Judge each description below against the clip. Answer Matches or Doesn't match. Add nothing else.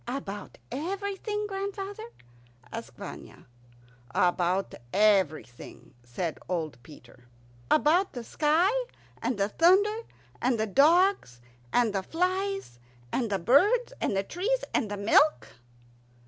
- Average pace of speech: Doesn't match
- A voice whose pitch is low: Doesn't match